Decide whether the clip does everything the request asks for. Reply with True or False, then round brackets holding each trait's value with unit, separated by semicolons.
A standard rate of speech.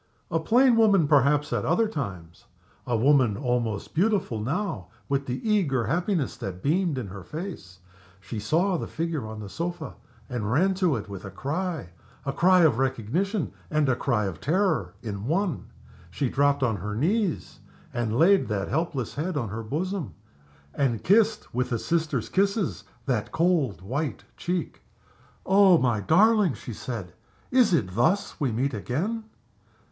True (160 wpm)